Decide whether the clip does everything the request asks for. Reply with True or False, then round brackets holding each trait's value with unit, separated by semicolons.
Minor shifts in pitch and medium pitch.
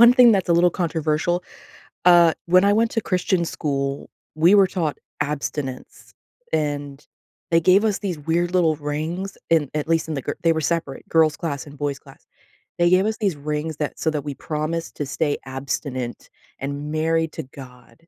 False (3.2 semitones; 160 Hz)